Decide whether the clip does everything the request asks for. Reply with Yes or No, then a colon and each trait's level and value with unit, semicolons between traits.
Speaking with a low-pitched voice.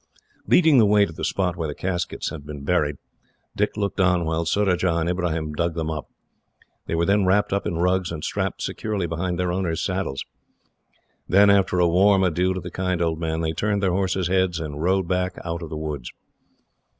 Yes: very low, 90 Hz